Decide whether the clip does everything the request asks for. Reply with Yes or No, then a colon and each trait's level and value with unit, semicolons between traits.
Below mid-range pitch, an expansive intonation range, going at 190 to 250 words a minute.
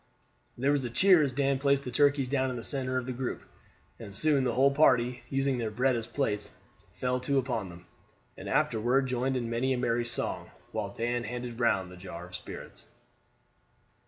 No: low, 125 Hz; narrow, 2.5 semitones; average, 195 wpm